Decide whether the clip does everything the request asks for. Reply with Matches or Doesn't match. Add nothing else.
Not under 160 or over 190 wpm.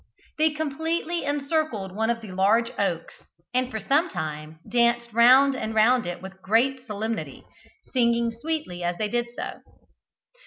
Doesn't match